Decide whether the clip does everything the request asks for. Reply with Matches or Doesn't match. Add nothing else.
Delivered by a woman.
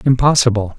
Doesn't match